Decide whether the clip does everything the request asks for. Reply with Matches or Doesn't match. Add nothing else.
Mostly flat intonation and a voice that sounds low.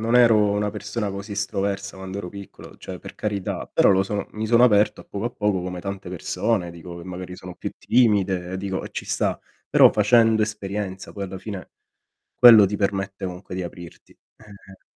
Matches